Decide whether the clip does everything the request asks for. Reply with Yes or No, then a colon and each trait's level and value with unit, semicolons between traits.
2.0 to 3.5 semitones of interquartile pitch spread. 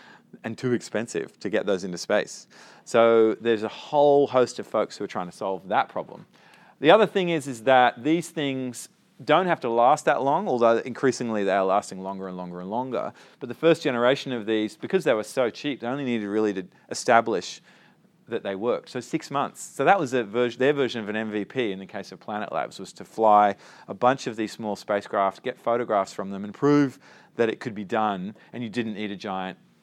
No: average, 4.1 semitones